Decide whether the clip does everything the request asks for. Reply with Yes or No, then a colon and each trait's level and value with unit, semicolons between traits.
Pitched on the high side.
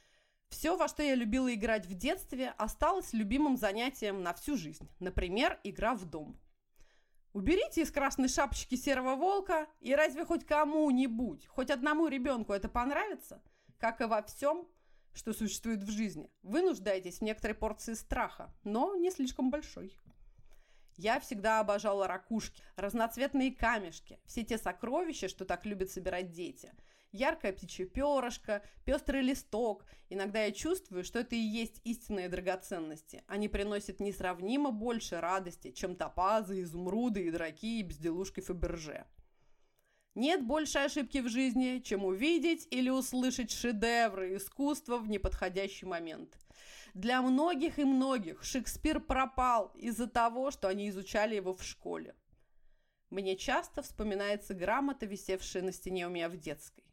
Yes: high, 230 Hz